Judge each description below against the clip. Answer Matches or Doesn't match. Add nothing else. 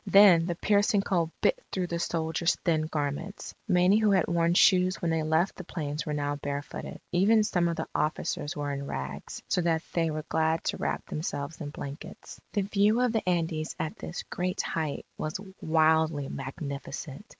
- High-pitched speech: Doesn't match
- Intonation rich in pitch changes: Doesn't match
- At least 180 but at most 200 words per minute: Matches